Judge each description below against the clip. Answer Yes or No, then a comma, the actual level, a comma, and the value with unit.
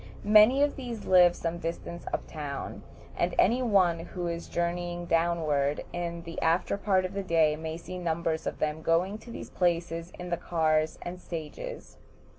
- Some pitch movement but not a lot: No, narrow, 1.9 semitones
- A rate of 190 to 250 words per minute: No, average, 175 wpm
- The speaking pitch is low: No, medium, 170 Hz